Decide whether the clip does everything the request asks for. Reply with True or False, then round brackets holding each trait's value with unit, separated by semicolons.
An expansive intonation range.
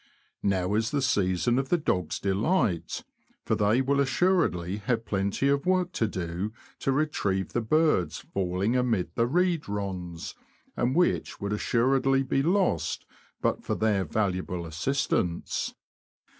True (6.4 semitones)